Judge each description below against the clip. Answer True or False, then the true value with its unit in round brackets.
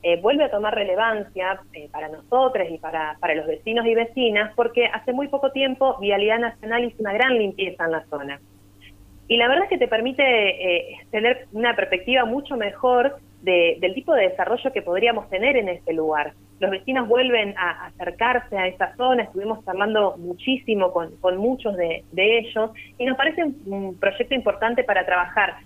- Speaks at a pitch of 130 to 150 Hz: False (215 Hz)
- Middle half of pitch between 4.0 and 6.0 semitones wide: True (5.3 semitones)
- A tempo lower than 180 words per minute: False (185 wpm)